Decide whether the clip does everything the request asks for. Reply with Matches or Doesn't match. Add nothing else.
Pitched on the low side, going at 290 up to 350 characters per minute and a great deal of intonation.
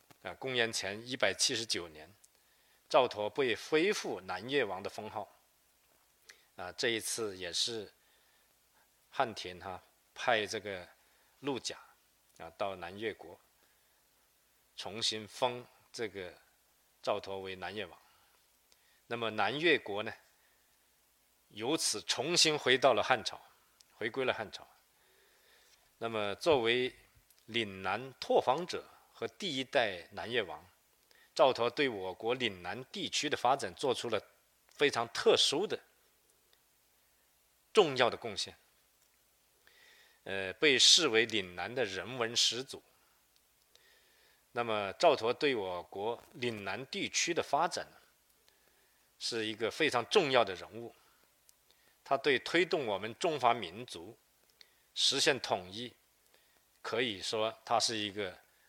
Doesn't match